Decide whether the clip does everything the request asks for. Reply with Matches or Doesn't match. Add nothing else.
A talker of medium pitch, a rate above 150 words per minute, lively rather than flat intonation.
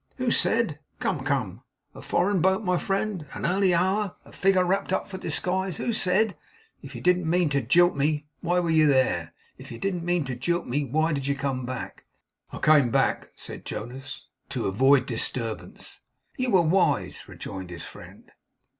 Matches